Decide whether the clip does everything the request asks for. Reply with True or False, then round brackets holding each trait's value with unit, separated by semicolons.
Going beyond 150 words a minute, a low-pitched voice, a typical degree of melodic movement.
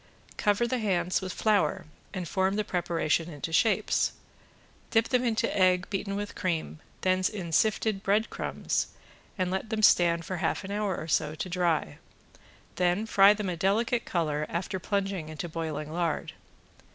False (160 wpm; 185 Hz; 3.5 semitones)